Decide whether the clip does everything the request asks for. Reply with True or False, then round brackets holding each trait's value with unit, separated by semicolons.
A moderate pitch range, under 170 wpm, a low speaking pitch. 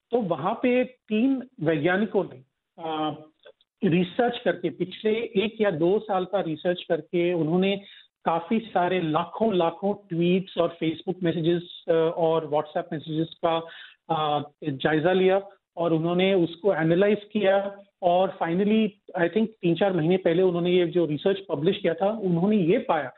False (3.1 semitones; 140 wpm; 180 Hz)